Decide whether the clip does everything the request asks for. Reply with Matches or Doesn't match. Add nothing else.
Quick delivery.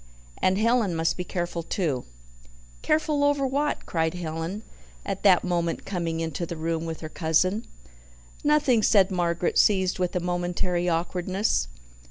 Doesn't match